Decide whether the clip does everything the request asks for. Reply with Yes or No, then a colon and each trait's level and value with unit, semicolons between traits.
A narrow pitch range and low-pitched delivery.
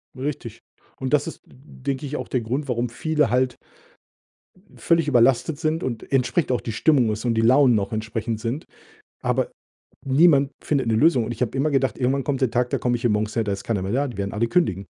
No: average, 3.6 semitones; low, 125 Hz